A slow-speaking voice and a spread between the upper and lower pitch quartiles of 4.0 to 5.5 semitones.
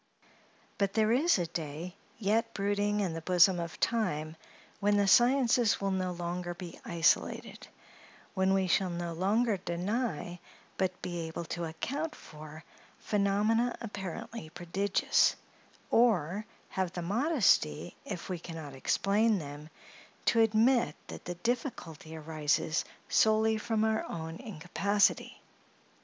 Yes: slow, 130 wpm; average, 4.6 semitones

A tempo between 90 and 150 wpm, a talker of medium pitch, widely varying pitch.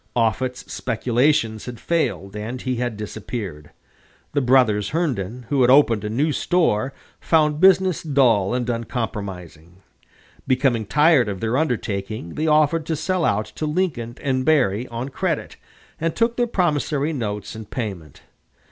No: average, 145 wpm; low, 125 Hz; wide, 5.9 semitones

